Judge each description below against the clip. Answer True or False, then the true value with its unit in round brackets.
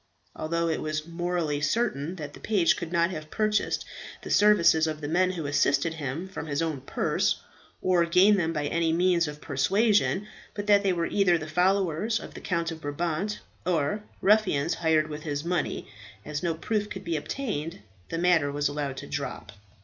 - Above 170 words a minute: True (190 wpm)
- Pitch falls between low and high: True (170 Hz)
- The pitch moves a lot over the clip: False (3.5 semitones)